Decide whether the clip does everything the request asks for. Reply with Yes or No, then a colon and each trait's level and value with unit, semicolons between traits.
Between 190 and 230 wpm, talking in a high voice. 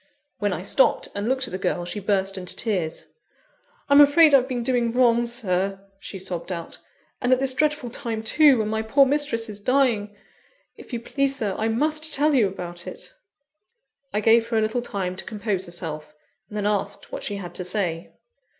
Yes: average, 195 wpm; high, 220 Hz